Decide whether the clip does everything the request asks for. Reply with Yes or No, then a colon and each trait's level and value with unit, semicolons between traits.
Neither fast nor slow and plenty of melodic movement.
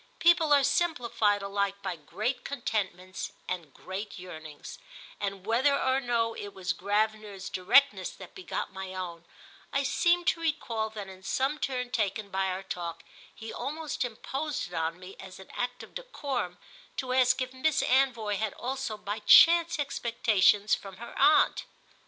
Yes: average, 160 wpm; wide, 6.0 semitones